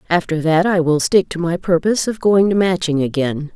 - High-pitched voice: No, medium, 170 Hz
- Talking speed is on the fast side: Yes, fast, 220 wpm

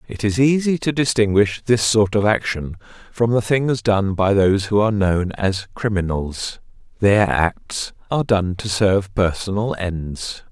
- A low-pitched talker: Yes, low, 105 Hz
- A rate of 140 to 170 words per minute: Yes, average, 160 wpm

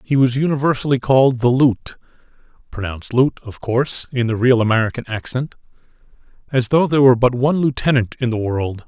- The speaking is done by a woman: No, male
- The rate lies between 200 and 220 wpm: No, average, 170 wpm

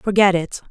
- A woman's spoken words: Yes, female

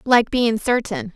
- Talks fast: No, average, 155 wpm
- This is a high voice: Yes, high, 235 Hz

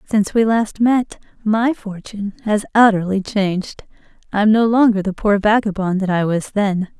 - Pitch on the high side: Yes, high, 205 Hz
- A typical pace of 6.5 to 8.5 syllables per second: No, 4.9 syllables/s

